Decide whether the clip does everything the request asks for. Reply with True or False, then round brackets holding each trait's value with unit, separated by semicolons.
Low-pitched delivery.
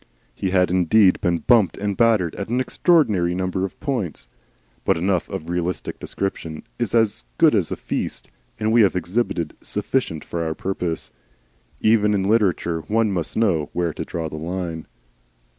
True (95 Hz)